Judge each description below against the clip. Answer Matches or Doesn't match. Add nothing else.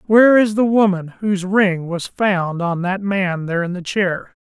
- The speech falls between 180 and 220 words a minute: Matches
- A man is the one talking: Matches